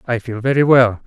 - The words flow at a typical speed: No, fast, 225 wpm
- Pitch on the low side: Yes, low, 120 Hz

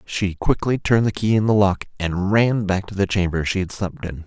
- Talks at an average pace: No, fast, 255 wpm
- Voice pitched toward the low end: Yes, low, 100 Hz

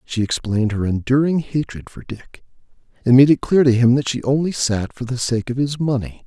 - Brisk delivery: Yes, fast, 220 wpm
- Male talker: Yes, male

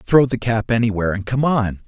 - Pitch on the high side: No, low, 115 Hz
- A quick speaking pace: Yes, fast, 225 wpm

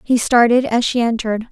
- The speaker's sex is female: Yes, female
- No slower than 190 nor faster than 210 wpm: Yes, average, 200 wpm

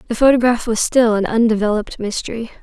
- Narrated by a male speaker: No, female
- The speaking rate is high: No, average, 160 wpm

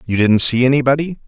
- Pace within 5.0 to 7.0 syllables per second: Yes, 6.3 syllables/s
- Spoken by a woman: No, male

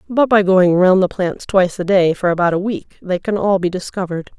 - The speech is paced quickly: Yes, fast, 245 wpm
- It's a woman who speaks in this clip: Yes, female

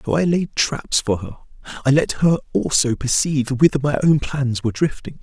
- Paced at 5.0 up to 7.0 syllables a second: Yes, 5.4 syllables/s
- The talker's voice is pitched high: No, medium, 140 Hz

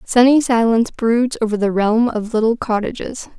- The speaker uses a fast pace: No, average, 160 wpm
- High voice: Yes, high, 230 Hz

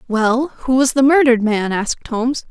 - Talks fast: No, average, 190 wpm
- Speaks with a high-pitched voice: Yes, high, 245 Hz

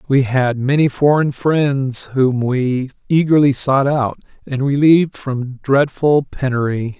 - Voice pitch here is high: No, low, 135 Hz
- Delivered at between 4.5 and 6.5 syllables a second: No, 3.7 syllables/s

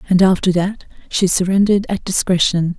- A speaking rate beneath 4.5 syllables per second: No, 5.4 syllables/s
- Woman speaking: Yes, female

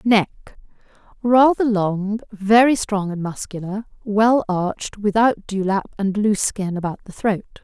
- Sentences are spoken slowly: Yes, slow, 125 wpm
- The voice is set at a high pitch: Yes, high, 205 Hz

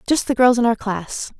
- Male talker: No, female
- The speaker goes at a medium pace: No, fast, 260 wpm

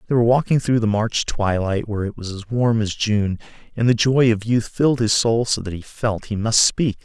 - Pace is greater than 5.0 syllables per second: Yes, 5.3 syllables/s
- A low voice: Yes, low, 110 Hz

